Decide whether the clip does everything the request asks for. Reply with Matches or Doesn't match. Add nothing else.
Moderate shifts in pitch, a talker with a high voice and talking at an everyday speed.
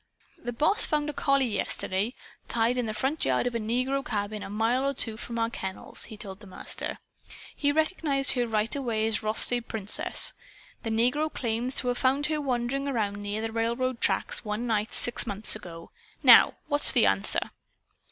Matches